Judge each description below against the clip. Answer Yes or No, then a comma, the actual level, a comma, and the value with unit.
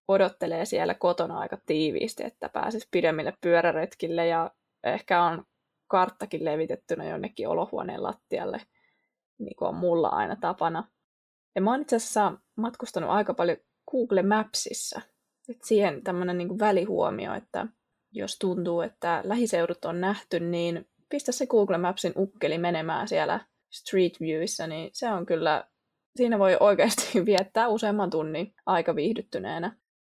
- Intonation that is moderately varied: Yes, average, 4.3 semitones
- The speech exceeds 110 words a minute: Yes, average, 135 wpm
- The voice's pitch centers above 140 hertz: Yes, medium, 185 Hz